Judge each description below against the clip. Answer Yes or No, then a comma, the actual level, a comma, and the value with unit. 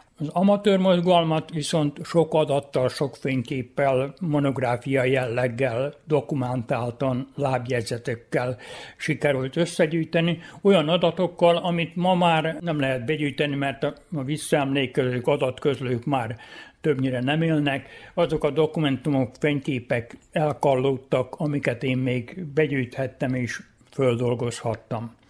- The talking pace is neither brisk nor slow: No, slow, 95 wpm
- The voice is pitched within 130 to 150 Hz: Yes, medium, 140 Hz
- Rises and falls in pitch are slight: No, average, 3.8 semitones